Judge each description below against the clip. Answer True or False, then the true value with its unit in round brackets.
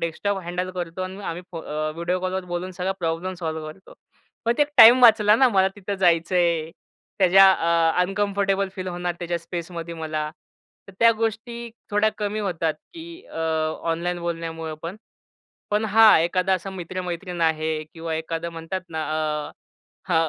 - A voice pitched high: False (180 Hz)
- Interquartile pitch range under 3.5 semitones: True (2.9 semitones)